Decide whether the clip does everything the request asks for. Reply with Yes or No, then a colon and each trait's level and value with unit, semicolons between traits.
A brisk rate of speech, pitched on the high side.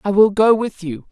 Yes: fast, 270 wpm; high, 195 Hz